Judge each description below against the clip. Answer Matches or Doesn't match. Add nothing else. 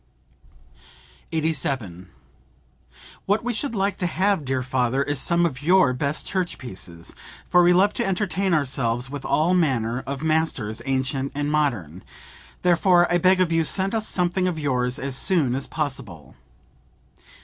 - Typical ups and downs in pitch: Doesn't match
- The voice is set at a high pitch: Doesn't match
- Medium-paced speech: Matches